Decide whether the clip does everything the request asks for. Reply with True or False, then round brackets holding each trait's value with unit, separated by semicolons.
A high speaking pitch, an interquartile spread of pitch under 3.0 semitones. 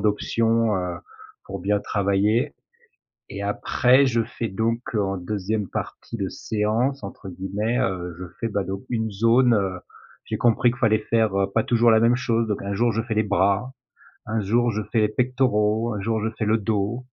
False (110 Hz; 2.6 semitones)